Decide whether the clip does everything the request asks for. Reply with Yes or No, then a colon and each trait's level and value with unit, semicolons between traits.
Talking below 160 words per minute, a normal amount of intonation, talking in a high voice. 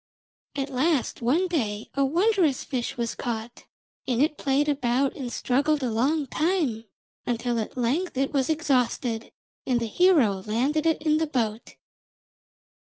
Yes: average, 150 wpm; average, 4.4 semitones; very high, 270 Hz